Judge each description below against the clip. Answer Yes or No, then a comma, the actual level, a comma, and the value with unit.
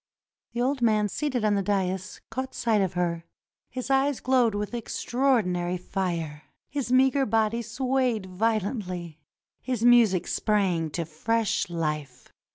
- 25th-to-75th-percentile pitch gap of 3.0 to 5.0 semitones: No, wide, 5.4 semitones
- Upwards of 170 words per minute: No, slow, 135 wpm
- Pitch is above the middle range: Yes, high, 215 Hz